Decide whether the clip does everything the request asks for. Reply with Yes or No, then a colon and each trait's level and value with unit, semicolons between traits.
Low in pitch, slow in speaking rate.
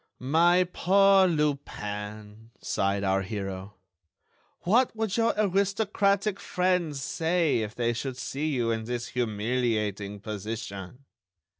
Yes: low, 125 Hz; slow, 110 wpm